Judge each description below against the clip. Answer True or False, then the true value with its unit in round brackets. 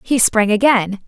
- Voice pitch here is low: False (225 Hz)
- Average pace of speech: True (170 wpm)